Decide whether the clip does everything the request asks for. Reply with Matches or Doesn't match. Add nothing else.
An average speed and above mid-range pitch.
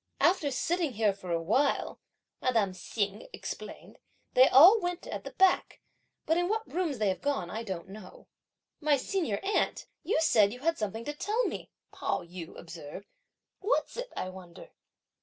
Matches